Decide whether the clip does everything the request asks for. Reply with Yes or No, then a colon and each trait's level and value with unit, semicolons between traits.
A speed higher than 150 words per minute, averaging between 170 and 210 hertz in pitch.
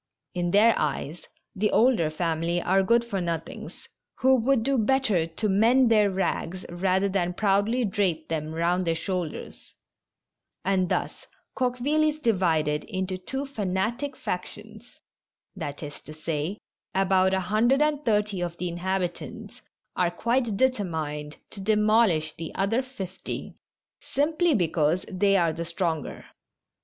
No: average, 140 wpm; high, 190 Hz